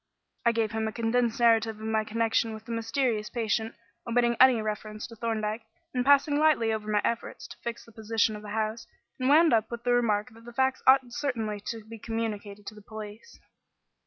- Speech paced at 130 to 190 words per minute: No, fast, 205 wpm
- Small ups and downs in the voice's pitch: Yes, narrow, 1.7 semitones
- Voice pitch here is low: No, high, 225 Hz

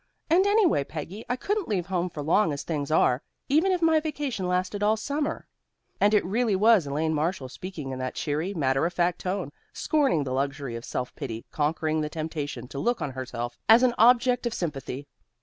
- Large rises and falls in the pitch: Yes, wide, 8.5 semitones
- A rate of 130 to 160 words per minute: No, average, 200 wpm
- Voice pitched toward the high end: No, medium, 175 Hz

